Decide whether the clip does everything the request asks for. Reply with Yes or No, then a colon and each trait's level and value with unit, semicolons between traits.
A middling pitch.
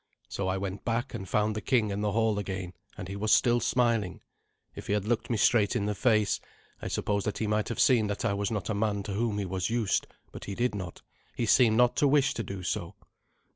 No: low, 105 Hz